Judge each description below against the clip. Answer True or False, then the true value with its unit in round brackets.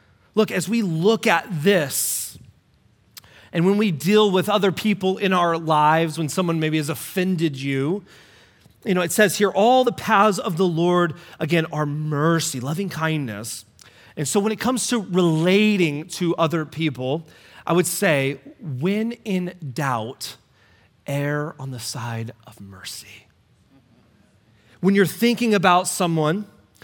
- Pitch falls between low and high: True (165 Hz)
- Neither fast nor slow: True (145 wpm)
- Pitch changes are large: True (6.1 semitones)